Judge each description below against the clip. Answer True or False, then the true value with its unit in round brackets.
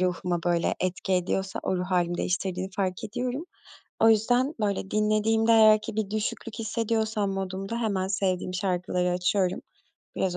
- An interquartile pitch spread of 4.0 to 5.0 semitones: False (3.1 semitones)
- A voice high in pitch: True (195 Hz)